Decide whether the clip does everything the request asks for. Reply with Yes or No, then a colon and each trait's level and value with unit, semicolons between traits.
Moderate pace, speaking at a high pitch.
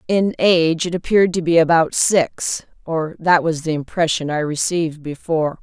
No: average, 160 wpm; medium, 165 Hz